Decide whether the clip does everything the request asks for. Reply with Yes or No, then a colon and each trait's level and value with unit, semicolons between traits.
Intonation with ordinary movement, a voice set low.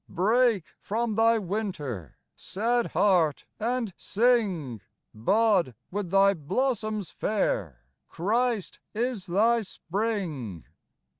No: average, 4.9 semitones; high, 205 Hz